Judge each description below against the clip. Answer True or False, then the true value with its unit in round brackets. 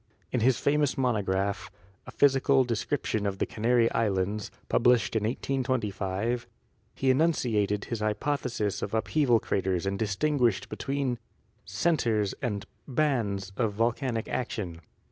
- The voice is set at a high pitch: False (115 Hz)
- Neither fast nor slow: False (120 wpm)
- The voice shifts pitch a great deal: False (4.3 semitones)